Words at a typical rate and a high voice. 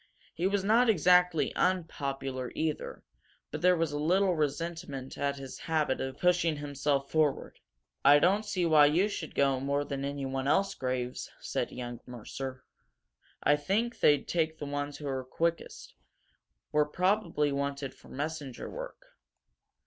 No: average, 150 wpm; medium, 150 Hz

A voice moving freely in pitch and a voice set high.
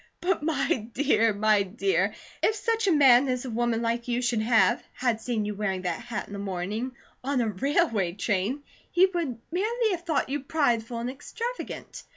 Yes: wide, 5.7 semitones; high, 245 Hz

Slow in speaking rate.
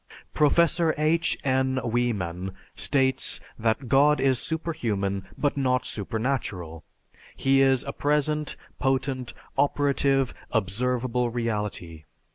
Yes: slow, 95 wpm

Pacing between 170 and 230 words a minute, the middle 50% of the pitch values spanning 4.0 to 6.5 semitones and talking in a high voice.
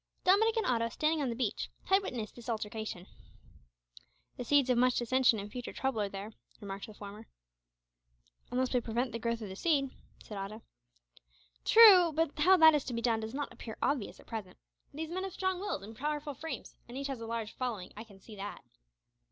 Yes: fast, 205 wpm; average, 5.3 semitones; high, 245 Hz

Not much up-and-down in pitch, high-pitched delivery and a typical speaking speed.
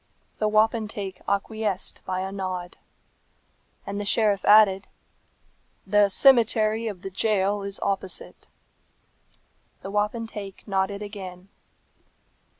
No: narrow, 1.9 semitones; high, 200 Hz; slow, 100 wpm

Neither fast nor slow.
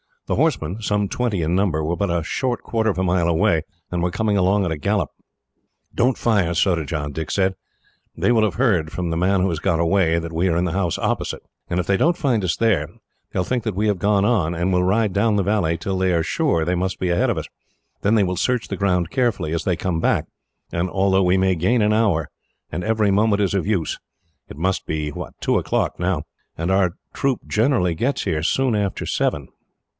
No: fast, 230 wpm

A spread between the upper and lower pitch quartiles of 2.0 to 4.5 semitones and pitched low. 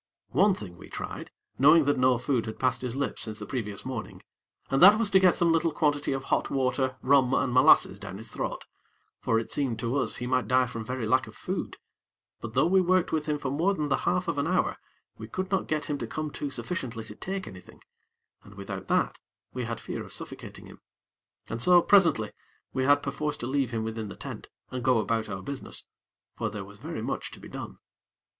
No: average, 5.1 semitones; low, 130 Hz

